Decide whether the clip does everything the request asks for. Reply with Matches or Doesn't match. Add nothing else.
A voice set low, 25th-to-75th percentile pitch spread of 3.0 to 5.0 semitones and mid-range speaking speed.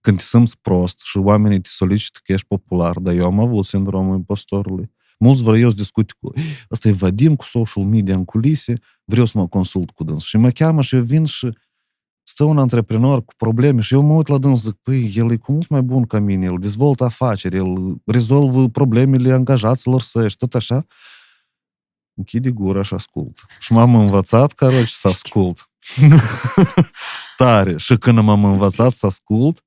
Doesn't match